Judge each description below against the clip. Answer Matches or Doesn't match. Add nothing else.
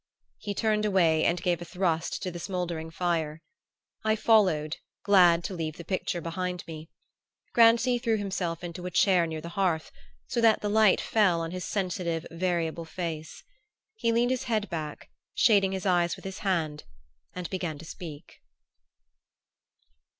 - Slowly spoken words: Doesn't match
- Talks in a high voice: Doesn't match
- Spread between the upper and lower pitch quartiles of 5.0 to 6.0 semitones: Doesn't match